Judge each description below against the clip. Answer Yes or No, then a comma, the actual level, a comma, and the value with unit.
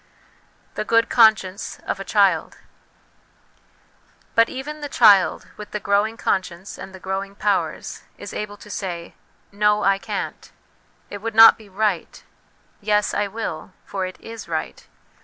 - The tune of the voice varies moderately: No, narrow, 2.3 semitones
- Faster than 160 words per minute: No, average, 155 wpm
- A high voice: Yes, high, 205 Hz